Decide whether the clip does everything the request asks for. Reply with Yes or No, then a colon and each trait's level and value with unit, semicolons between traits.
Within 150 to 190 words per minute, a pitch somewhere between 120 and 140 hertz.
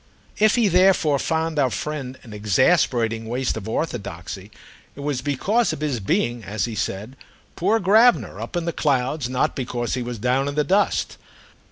Yes: average, 175 wpm; low, 135 Hz